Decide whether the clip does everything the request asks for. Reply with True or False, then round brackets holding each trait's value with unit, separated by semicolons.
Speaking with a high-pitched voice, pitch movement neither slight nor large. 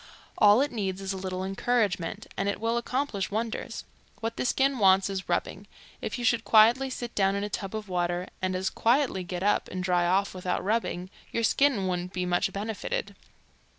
True (200 Hz; 3.7 semitones)